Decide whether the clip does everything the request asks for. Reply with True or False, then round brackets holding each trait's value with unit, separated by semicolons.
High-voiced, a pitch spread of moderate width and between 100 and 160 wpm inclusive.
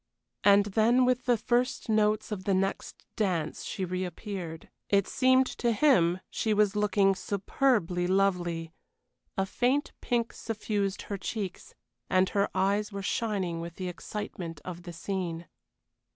True (200 Hz; 3.0 semitones; 140 wpm)